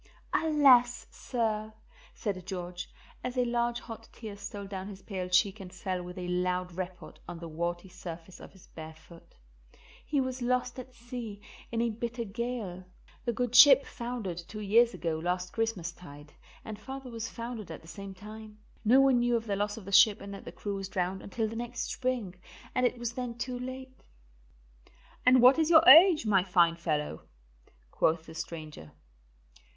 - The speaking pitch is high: Yes, high, 210 Hz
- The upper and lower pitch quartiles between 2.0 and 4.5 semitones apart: No, average, 5.0 semitones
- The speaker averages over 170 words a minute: Yes, average, 180 wpm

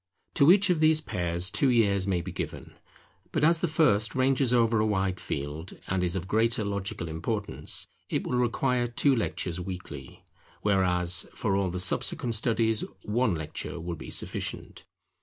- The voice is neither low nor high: No, low, 105 Hz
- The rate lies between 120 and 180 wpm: Yes, average, 165 wpm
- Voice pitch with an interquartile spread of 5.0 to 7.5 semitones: Yes, wide, 5.5 semitones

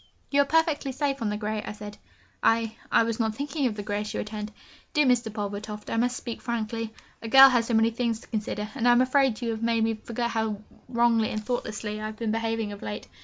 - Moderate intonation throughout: No, narrow, 2.3 semitones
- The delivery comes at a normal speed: No, fast, 240 wpm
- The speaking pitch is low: No, high, 225 Hz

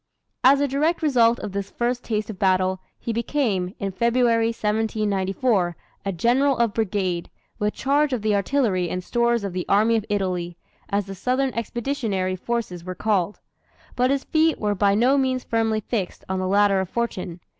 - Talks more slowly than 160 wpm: No, average, 175 wpm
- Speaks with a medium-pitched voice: No, high, 215 Hz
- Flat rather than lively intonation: No, average, 4.1 semitones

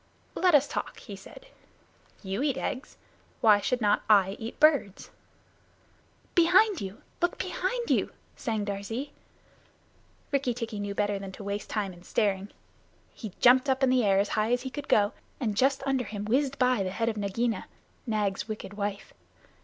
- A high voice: Yes, high, 225 Hz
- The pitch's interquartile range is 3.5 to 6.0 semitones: Yes, average, 4.7 semitones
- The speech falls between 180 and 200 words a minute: No, average, 170 wpm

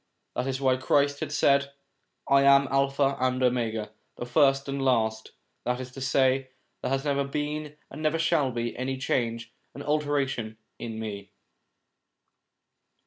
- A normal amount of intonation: No, narrow, 2.2 semitones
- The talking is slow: No, average, 165 wpm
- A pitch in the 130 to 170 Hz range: Yes, low, 135 Hz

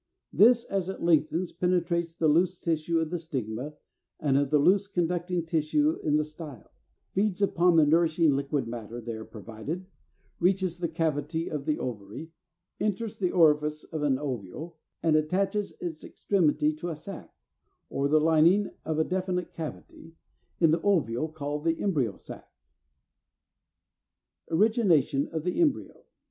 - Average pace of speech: Yes, average, 150 wpm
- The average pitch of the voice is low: No, medium, 160 Hz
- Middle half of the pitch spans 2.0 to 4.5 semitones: Yes, average, 3.3 semitones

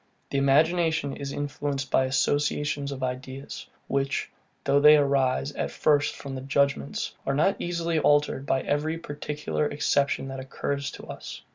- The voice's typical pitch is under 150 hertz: Yes, medium, 140 Hz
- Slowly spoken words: No, average, 150 wpm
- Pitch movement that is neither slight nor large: No, narrow, 1.4 semitones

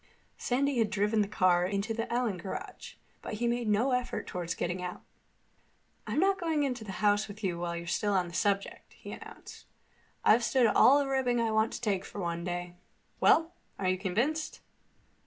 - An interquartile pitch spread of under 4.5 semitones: No, average, 4.8 semitones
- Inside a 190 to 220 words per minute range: Yes, average, 195 wpm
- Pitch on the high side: Yes, high, 210 Hz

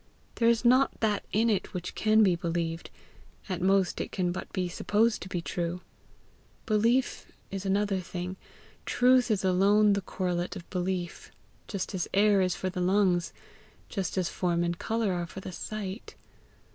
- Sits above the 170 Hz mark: Yes, high, 190 Hz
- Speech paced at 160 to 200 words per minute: Yes, average, 170 wpm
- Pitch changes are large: No, average, 3.0 semitones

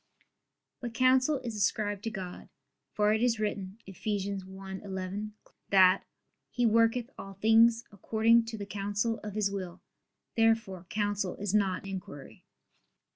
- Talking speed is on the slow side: Yes, slow, 130 wpm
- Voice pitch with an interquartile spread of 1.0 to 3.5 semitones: Yes, average, 2.7 semitones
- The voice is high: Yes, high, 205 Hz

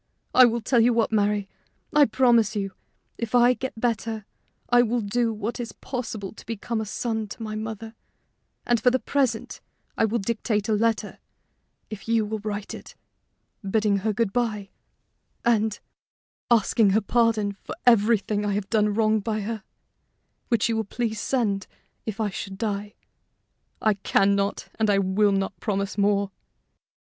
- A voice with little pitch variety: Yes, narrow, 2.2 semitones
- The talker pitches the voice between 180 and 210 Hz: No, high, 220 Hz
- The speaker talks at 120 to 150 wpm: No, average, 165 wpm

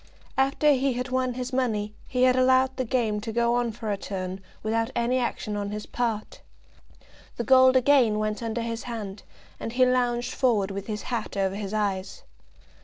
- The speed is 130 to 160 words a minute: No, average, 185 wpm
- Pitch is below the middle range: No, high, 235 Hz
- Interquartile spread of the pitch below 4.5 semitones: Yes, average, 3.2 semitones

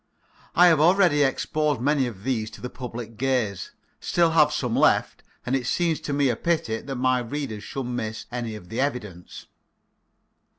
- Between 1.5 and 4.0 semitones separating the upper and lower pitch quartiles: No, average, 4.4 semitones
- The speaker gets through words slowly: No, average, 175 wpm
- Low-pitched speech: Yes, low, 130 Hz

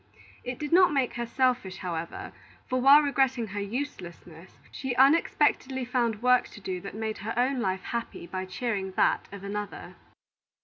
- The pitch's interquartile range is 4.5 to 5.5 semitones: Yes, average, 5.2 semitones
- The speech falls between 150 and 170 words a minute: Yes, average, 165 wpm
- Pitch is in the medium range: No, high, 235 Hz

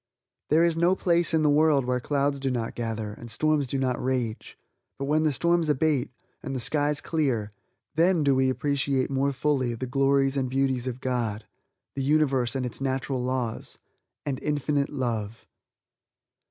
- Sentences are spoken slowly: No, average, 170 wpm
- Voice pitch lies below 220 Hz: Yes, low, 135 Hz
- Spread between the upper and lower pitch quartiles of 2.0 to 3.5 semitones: Yes, average, 2.9 semitones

